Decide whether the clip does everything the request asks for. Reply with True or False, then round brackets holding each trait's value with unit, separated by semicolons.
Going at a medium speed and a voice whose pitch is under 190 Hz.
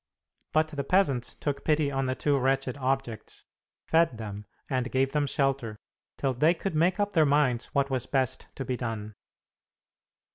True (170 wpm; 135 Hz)